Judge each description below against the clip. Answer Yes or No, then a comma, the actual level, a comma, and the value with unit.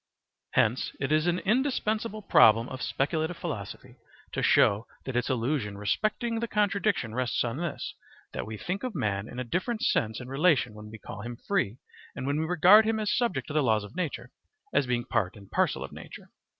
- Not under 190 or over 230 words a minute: Yes, average, 200 wpm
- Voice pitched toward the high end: No, medium, 140 Hz